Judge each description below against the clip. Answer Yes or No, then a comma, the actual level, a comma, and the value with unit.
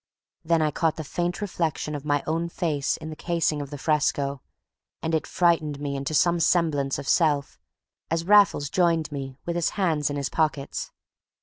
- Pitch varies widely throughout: No, average, 2.8 semitones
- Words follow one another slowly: No, average, 185 wpm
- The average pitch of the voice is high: No, medium, 155 Hz